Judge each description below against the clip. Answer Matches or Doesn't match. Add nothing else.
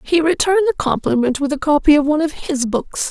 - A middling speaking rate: Doesn't match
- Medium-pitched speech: Doesn't match